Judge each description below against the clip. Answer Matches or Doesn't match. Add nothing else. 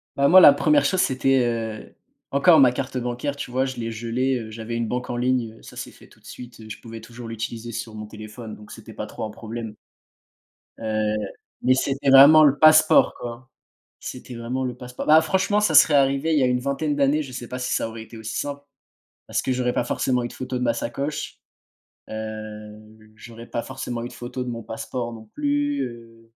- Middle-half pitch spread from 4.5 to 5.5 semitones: Doesn't match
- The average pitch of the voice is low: Matches